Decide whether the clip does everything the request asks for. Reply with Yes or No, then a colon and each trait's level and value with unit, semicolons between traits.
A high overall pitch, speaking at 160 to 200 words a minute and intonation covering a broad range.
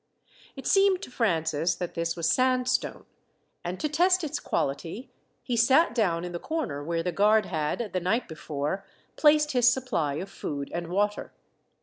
Yes: high, 200 Hz; average, 165 wpm; wide, 7.5 semitones